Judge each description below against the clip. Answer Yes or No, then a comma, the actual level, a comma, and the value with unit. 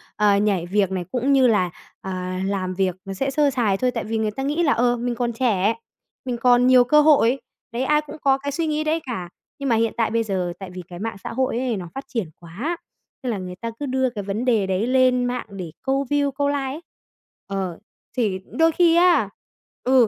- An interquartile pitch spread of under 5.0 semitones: No, wide, 5.5 semitones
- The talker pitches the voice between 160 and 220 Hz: No, high, 240 Hz